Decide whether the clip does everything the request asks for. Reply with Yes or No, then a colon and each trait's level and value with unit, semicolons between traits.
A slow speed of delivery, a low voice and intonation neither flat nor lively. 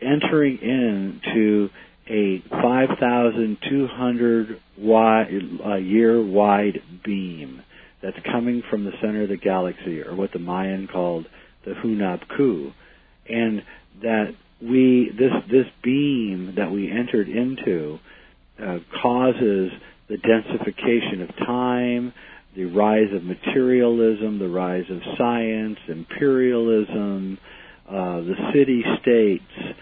Yes: slow, 100 wpm; low, 110 Hz; average, 3.9 semitones